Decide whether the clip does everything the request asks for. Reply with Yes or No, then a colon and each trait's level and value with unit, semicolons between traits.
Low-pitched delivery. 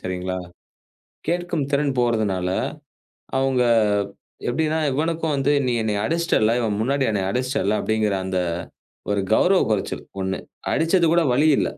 Yes: low, 125 Hz